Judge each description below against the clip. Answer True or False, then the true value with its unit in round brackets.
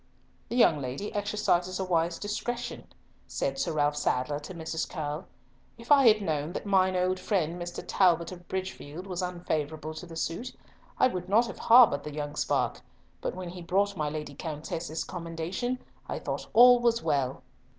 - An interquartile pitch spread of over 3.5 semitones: True (4.4 semitones)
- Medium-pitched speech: True (175 Hz)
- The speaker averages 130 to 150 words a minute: False (175 wpm)